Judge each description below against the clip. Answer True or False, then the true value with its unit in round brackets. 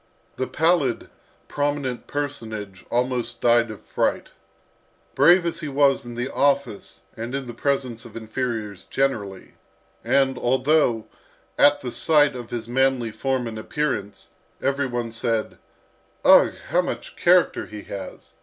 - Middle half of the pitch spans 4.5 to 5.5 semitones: False (3.3 semitones)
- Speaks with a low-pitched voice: True (125 Hz)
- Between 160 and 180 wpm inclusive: False (135 wpm)